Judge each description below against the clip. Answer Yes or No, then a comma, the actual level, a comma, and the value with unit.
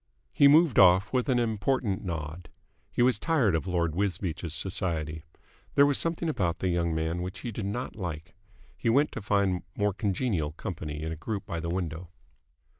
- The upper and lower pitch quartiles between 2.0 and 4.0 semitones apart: No, wide, 5.4 semitones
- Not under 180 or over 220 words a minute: Yes, average, 185 wpm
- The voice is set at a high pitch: No, very low, 95 Hz